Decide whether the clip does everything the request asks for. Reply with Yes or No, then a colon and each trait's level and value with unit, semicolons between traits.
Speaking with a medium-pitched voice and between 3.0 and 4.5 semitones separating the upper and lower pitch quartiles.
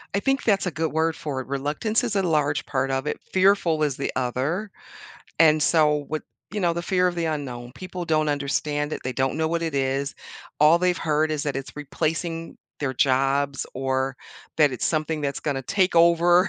Yes: medium, 155 Hz; average, 3.5 semitones